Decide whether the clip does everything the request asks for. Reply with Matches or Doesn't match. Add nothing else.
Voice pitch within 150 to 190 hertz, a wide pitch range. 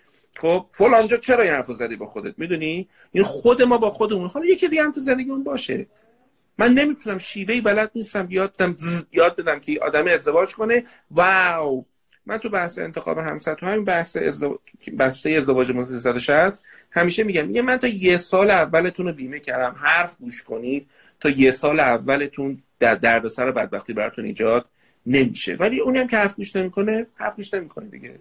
Matches